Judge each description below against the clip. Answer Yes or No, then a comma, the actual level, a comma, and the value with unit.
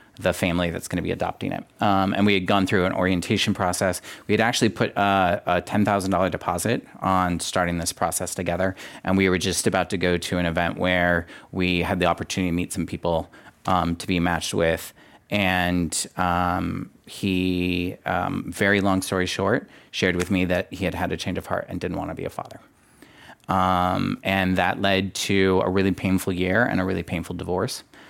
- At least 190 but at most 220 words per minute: Yes, average, 200 wpm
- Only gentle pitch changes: Yes, narrow, 1.5 semitones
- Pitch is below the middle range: Yes, very low, 90 Hz